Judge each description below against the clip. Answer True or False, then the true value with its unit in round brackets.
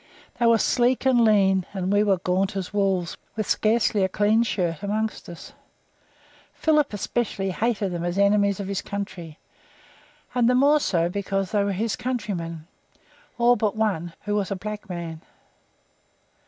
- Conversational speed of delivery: True (160 wpm)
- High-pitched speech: True (200 Hz)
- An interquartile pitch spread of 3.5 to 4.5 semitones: False (2.9 semitones)